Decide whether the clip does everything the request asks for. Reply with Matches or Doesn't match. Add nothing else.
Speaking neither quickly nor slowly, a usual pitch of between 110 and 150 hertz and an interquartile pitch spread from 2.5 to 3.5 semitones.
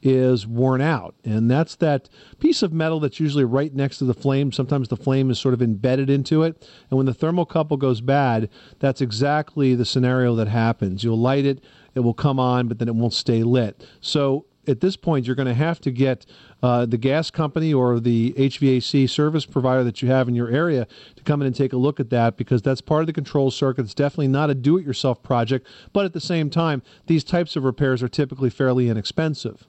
Doesn't match